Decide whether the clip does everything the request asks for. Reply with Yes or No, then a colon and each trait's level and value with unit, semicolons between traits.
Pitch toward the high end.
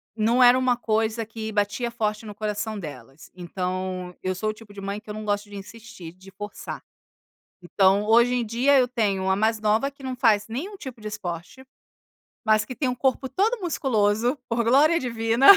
Yes: high, 220 Hz